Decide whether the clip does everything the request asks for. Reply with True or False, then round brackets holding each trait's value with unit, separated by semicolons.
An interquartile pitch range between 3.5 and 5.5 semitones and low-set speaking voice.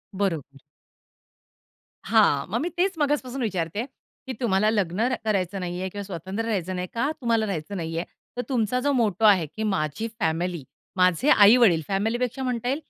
False (4.7 semitones; 205 Hz)